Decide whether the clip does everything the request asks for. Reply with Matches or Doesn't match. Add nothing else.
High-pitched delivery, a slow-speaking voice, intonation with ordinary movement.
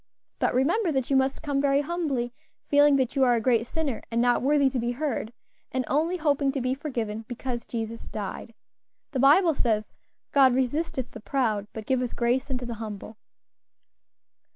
Doesn't match